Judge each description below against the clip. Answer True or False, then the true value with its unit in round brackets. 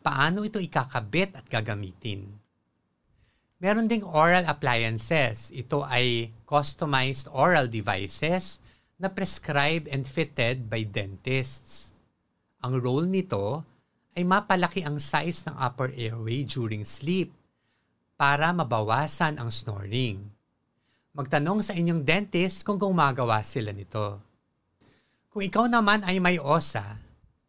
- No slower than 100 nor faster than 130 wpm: True (110 wpm)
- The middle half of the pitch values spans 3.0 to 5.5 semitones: False (7.3 semitones)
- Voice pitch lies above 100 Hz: True (140 Hz)